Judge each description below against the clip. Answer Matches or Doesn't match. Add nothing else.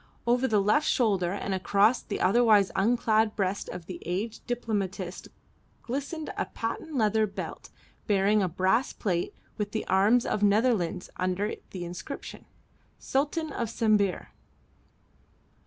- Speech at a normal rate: Doesn't match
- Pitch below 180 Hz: Doesn't match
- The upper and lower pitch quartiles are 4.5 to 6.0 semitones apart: Doesn't match